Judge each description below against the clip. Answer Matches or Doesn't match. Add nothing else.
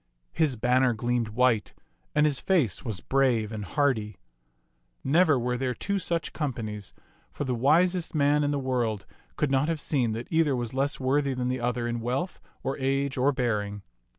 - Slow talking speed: Doesn't match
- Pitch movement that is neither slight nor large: Matches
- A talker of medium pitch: Doesn't match